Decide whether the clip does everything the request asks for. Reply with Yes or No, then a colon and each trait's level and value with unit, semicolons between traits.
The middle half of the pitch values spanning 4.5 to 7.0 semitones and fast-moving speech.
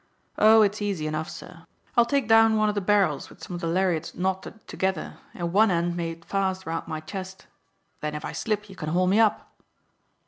No: average, 3.8 semitones; fast, 210 wpm